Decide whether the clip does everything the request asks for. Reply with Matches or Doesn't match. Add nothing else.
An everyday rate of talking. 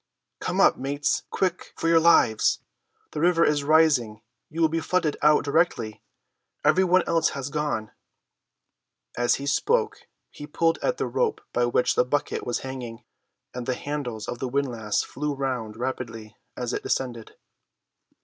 Matches